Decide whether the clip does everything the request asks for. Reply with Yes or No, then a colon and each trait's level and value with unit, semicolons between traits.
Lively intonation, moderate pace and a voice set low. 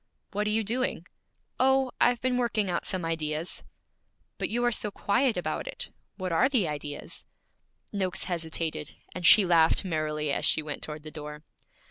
No: wide, 6.2 semitones; average, 170 wpm; medium, 180 Hz